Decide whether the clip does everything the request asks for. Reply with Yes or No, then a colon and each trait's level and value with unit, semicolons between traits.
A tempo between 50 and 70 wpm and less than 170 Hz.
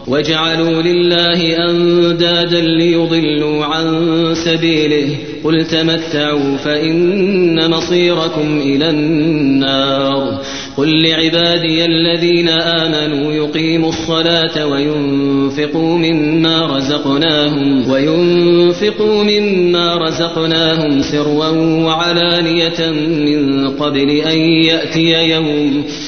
Yes: slow, 65 wpm; medium, 160 Hz